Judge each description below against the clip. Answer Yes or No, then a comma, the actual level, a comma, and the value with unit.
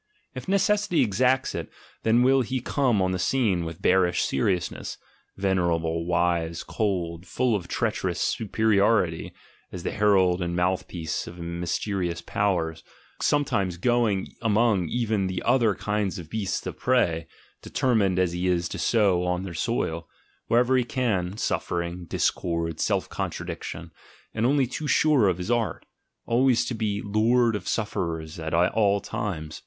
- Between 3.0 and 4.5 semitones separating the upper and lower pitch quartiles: No, average, 5.0 semitones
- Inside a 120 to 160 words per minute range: Yes, average, 150 wpm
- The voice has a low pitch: Yes, very low, 95 Hz